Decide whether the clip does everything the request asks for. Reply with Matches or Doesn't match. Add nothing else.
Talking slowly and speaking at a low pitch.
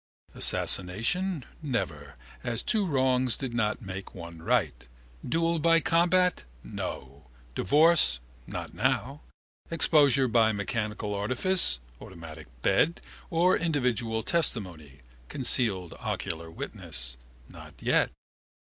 Matches